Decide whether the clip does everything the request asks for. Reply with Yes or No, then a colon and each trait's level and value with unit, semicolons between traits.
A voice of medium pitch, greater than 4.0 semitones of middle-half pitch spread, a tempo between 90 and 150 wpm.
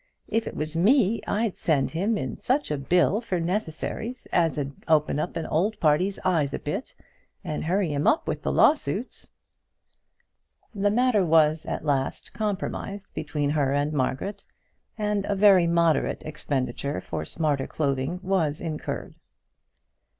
Yes: medium, 170 Hz; average, 5.3 semitones; average, 145 wpm